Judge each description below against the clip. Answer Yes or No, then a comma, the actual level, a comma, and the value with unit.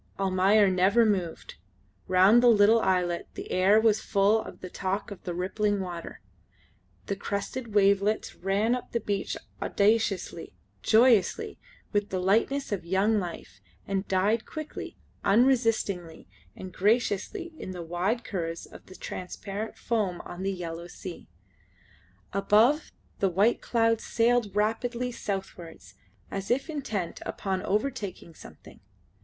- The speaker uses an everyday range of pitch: Yes, average, 3.4 semitones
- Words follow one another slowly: Yes, slow, 130 wpm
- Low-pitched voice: No, high, 200 Hz